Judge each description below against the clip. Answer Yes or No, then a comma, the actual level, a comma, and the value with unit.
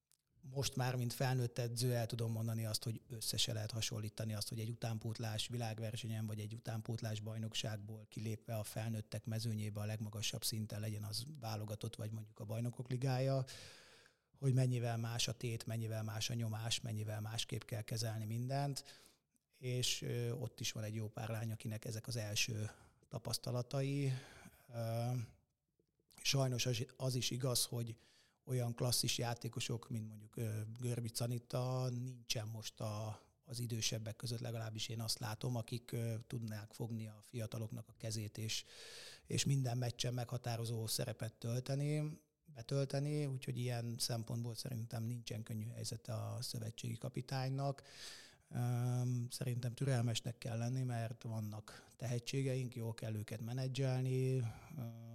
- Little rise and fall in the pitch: Yes, narrow, 2.1 semitones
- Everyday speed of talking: Yes, average, 130 wpm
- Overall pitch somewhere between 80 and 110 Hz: No, low, 120 Hz